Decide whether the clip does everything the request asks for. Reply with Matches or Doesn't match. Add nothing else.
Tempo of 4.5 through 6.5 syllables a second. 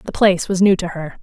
Matches